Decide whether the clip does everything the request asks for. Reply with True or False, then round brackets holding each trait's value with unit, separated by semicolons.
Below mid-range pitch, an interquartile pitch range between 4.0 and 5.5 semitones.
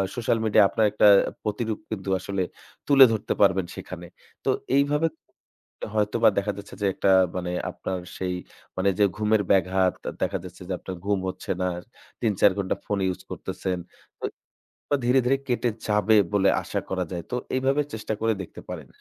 False (105 Hz; 3.1 semitones)